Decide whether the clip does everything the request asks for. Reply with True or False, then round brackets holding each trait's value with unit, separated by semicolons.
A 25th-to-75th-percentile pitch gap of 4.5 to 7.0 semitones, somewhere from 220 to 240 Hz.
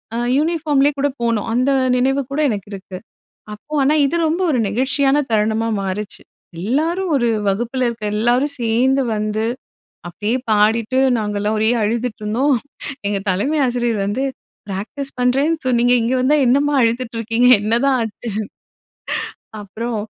False (4.1 semitones; 235 Hz)